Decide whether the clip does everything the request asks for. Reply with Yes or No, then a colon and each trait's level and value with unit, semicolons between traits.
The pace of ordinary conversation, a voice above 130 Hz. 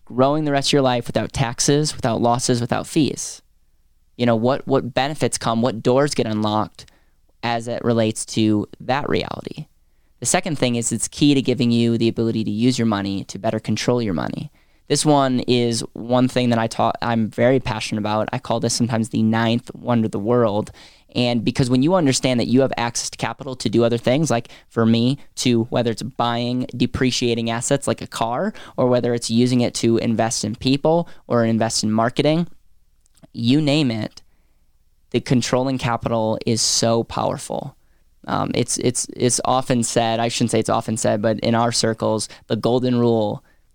No: average, 190 wpm; low, 120 Hz